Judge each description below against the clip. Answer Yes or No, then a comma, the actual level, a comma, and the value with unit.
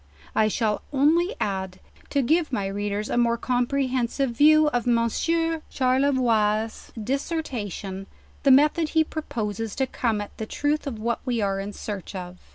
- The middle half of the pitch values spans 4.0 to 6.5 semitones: Yes, average, 5.3 semitones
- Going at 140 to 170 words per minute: Yes, average, 160 wpm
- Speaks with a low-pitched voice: No, high, 240 Hz